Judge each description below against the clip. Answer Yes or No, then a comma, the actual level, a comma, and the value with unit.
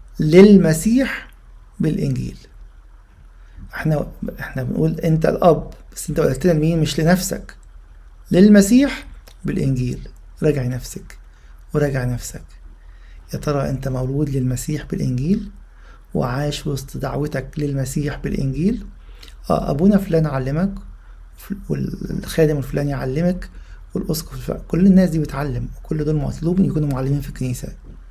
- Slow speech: Yes, slow, 105 wpm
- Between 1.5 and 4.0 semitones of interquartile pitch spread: No, average, 4.7 semitones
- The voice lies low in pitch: No, medium, 145 Hz